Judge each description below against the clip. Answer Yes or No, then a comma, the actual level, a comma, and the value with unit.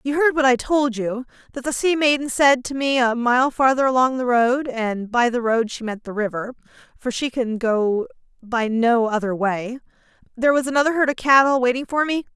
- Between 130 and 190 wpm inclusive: No, fast, 205 wpm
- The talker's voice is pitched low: No, very high, 260 Hz